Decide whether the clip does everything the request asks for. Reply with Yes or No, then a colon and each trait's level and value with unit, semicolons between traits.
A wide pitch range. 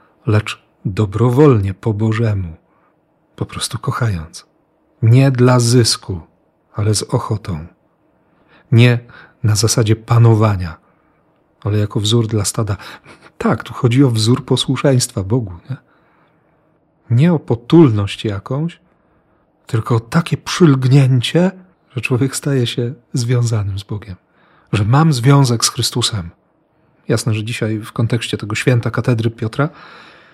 No: average, 4.2 semitones